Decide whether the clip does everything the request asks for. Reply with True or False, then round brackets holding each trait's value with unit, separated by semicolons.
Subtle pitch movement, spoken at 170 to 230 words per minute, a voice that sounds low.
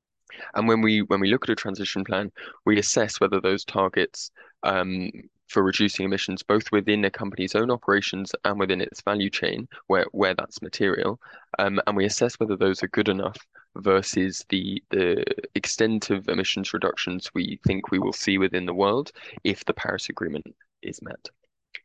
True (2.0 semitones; 175 wpm; 100 Hz)